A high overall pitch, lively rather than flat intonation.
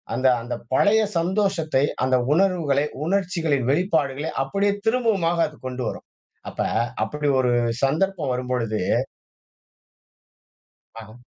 No: medium, 155 Hz; wide, 6.4 semitones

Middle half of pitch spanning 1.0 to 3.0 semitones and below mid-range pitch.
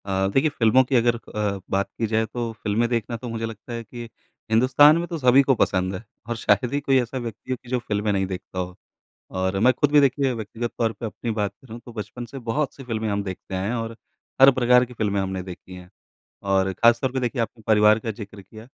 No: average, 3.5 semitones; low, 115 Hz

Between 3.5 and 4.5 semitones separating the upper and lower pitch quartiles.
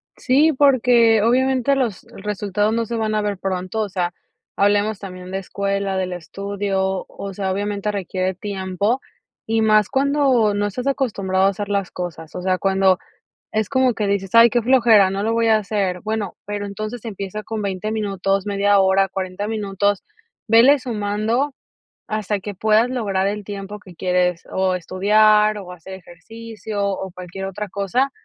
No: narrow, 2.6 semitones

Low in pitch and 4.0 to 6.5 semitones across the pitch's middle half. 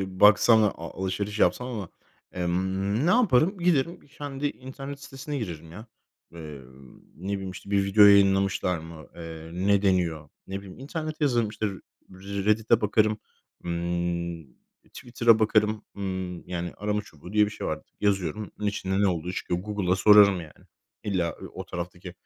No: low, 100 Hz; average, 3.5 semitones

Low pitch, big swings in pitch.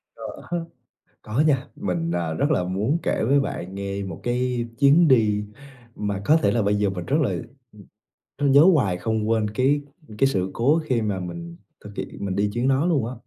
Yes: low, 115 Hz; wide, 5.8 semitones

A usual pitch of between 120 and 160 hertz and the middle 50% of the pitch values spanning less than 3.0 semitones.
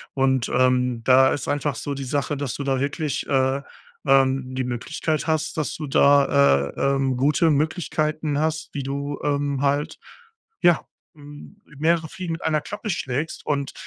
Yes: medium, 140 Hz; narrow, 2.5 semitones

